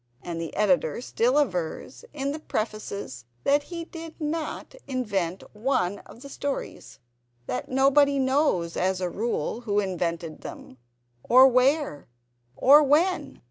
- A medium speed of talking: No, slow, 130 wpm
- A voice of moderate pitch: No, high, 245 Hz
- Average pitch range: No, wide, 7.7 semitones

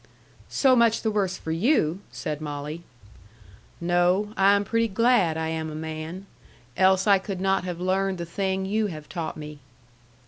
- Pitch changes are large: No, average, 3.9 semitones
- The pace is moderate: Yes, average, 170 wpm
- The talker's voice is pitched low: No, medium, 185 Hz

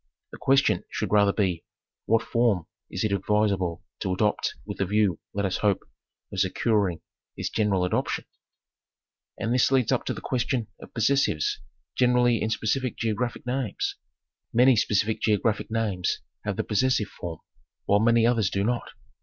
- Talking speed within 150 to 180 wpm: Yes, average, 155 wpm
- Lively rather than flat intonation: No, average, 3.3 semitones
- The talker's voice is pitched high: No, low, 110 Hz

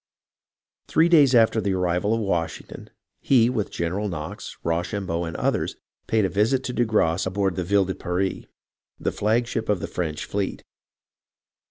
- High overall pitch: No, low, 100 Hz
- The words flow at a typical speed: Yes, average, 165 wpm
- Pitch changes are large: No, average, 4.1 semitones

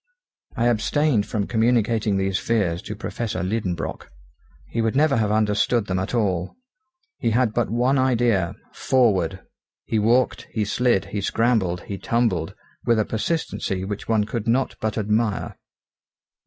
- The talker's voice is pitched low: Yes, low, 110 Hz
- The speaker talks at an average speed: Yes, average, 145 wpm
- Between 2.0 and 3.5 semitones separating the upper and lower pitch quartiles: Yes, average, 3.2 semitones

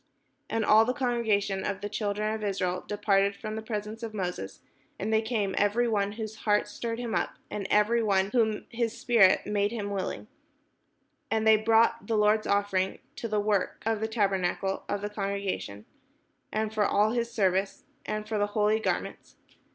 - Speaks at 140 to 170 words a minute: No, average, 185 wpm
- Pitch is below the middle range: No, high, 210 Hz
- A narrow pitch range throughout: Yes, narrow, 1.8 semitones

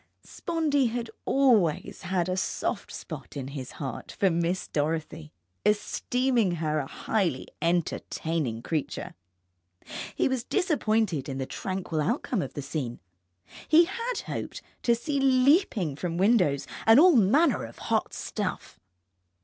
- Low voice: No, high, 190 Hz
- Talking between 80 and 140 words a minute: Yes, slow, 135 wpm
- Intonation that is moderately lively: No, wide, 8.5 semitones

